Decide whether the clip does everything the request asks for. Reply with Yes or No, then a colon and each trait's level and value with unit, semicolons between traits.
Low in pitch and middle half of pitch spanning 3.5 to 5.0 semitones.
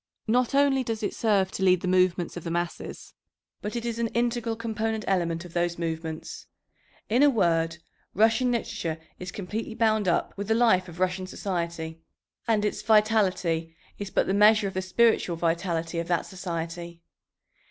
No: high, 190 Hz; average, 4.5 semitones